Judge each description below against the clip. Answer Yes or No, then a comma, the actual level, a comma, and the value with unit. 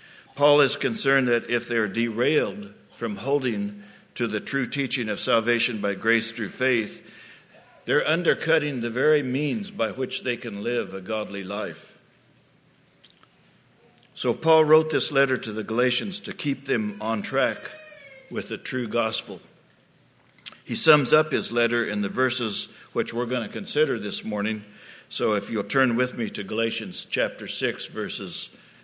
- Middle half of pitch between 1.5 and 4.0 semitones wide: No, average, 4.5 semitones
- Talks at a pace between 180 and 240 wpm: No, average, 160 wpm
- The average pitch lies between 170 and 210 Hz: No, low, 120 Hz